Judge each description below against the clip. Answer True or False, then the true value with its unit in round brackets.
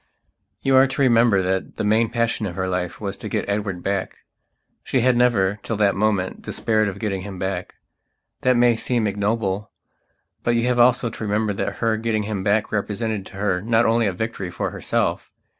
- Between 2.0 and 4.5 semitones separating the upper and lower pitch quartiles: True (3.0 semitones)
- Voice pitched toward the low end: True (110 Hz)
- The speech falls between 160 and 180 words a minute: False (195 wpm)